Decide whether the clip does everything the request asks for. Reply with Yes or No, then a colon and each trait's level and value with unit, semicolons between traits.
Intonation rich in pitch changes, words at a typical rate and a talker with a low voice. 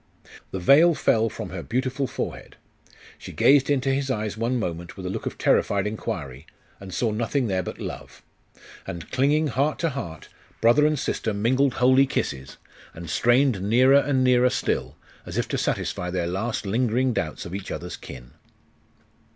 Yes: wide, 6.2 semitones; average, 170 wpm; low, 115 Hz